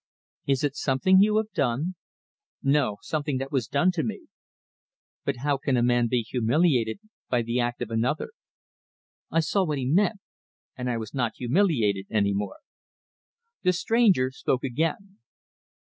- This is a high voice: No, low, 135 Hz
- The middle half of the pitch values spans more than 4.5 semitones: Yes, wide, 5.5 semitones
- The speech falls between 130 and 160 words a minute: Yes, average, 155 wpm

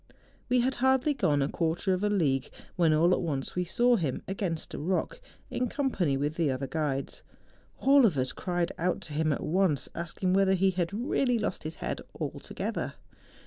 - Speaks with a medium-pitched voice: Yes, medium, 175 Hz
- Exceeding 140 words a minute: Yes, average, 190 wpm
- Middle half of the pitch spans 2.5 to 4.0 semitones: No, average, 5.1 semitones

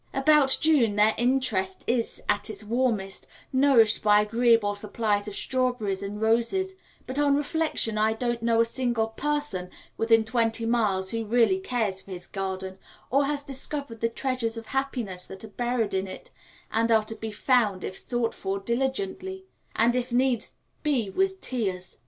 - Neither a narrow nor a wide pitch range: Yes, average, 3.8 semitones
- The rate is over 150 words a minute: Yes, average, 165 wpm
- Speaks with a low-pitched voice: No, high, 230 Hz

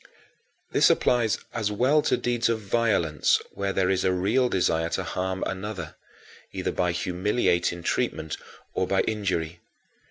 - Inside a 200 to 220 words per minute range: No, average, 150 wpm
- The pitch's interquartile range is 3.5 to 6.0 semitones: Yes, average, 3.9 semitones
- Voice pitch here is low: Yes, very low, 95 Hz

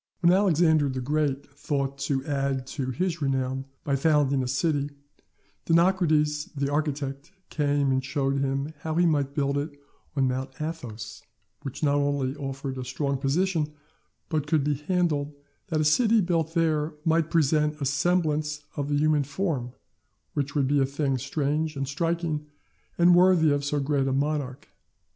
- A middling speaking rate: Yes, average, 160 wpm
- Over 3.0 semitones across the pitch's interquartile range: No, narrow, 2.5 semitones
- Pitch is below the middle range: No, medium, 145 Hz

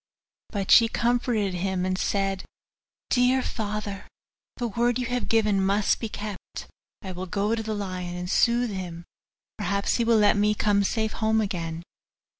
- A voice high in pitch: Yes, high, 205 Hz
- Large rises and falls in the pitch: No, average, 3.1 semitones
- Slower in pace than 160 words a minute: No, average, 165 wpm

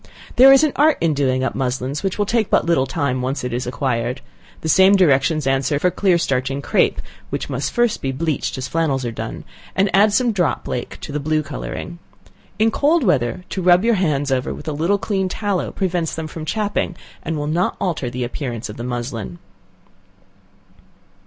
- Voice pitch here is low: No, medium, 155 Hz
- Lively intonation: Yes, wide, 6.4 semitones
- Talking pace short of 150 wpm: No, average, 200 wpm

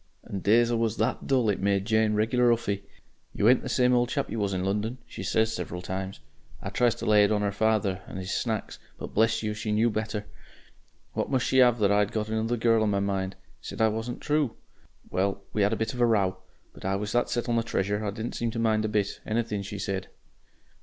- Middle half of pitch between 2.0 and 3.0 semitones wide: Yes, narrow, 2.4 semitones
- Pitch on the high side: No, low, 110 Hz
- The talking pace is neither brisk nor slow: No, fast, 240 wpm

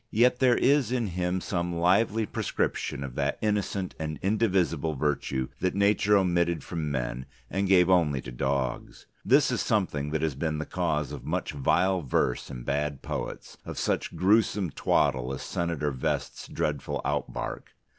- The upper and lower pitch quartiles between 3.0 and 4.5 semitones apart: No, average, 5.3 semitones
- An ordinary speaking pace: Yes, average, 160 wpm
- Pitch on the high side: No, very low, 85 Hz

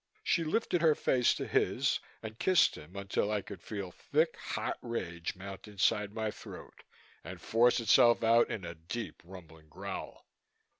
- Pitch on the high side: No, low, 105 Hz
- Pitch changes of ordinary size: Yes, average, 4.4 semitones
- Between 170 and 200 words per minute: No, average, 160 wpm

